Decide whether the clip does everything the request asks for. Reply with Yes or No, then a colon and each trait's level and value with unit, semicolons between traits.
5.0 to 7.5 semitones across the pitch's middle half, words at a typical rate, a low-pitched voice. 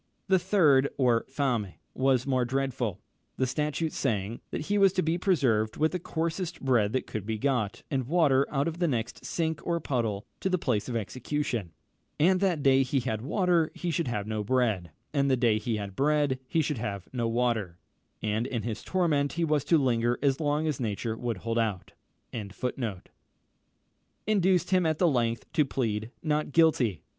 Yes: wide, 5.4 semitones; average, 165 wpm; low, 130 Hz